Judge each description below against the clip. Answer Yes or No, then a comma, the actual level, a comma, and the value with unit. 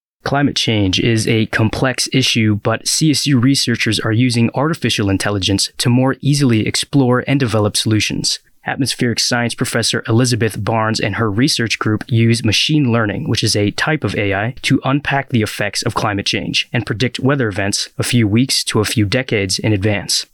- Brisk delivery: No, average, 170 wpm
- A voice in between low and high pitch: No, low, 115 Hz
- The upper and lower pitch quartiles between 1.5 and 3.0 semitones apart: No, average, 3.4 semitones